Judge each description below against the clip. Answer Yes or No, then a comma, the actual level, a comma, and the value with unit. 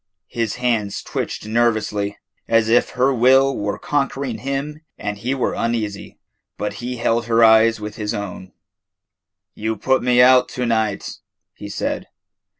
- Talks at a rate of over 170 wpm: No, average, 150 wpm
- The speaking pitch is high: No, low, 115 Hz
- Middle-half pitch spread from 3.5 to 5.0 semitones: No, average, 3.0 semitones